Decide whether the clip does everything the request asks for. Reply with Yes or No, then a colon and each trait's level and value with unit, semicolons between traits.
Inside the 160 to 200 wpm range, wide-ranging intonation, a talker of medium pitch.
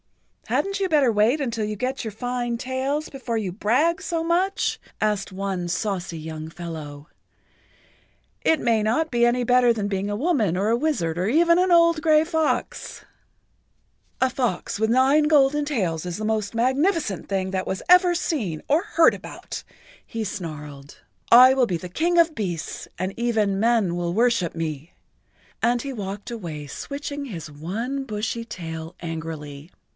No: average, 165 wpm; wide, 7.5 semitones; high, 225 Hz